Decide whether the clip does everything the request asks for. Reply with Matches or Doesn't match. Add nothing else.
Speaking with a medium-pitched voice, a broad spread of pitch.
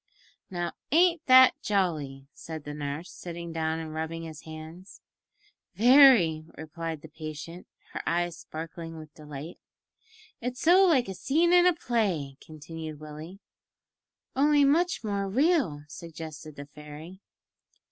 Matches